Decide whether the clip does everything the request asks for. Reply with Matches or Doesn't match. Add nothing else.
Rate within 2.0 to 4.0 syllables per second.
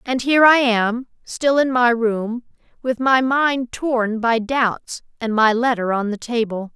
Matches